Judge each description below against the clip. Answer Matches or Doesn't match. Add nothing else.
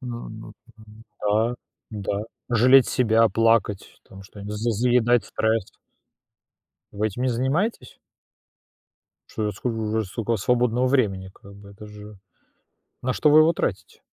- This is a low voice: Matches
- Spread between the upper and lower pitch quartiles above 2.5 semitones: Matches